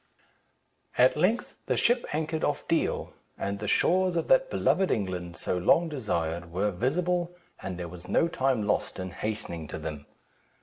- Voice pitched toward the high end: No, low, 110 Hz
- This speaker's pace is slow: No, average, 165 wpm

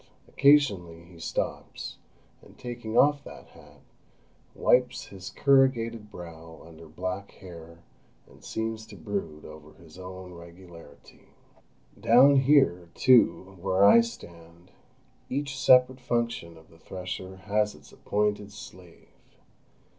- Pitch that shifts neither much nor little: No, wide, 6.1 semitones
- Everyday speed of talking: No, slow, 115 wpm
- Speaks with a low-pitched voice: Yes, very low, 95 Hz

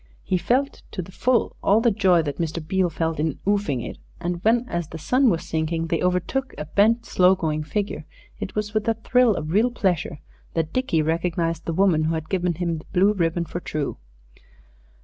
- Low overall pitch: No, medium, 175 Hz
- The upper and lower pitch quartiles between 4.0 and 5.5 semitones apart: Yes, average, 4.4 semitones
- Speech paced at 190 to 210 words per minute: Yes, fast, 205 wpm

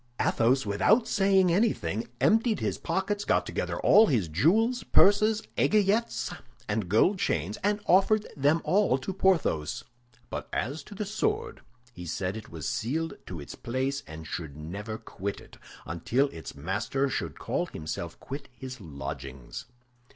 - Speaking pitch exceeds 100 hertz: Yes, low, 135 Hz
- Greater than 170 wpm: No, average, 145 wpm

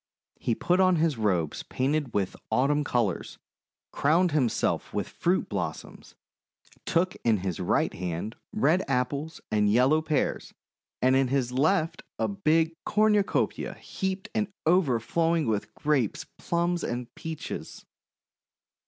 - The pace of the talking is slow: Yes, slow, 125 wpm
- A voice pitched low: No, medium, 150 Hz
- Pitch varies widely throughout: Yes, wide, 6.2 semitones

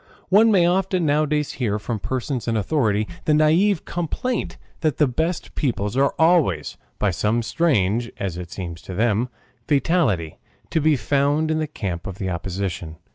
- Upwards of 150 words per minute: Yes, average, 165 wpm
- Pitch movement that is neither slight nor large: No, wide, 7.9 semitones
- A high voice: No, low, 130 Hz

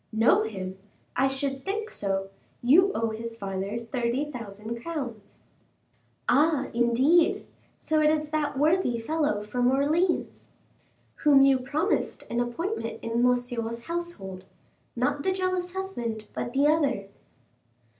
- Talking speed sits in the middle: No, slow, 125 wpm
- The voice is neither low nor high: No, very high, 255 Hz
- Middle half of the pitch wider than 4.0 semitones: Yes, average, 5.2 semitones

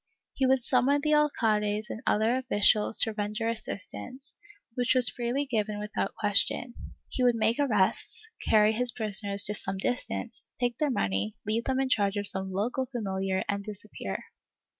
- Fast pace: No, average, 160 wpm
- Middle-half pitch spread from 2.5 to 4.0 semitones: Yes, average, 3.5 semitones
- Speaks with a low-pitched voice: No, high, 220 Hz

